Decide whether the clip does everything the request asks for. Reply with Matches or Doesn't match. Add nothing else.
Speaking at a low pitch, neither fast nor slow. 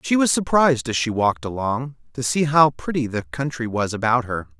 Doesn't match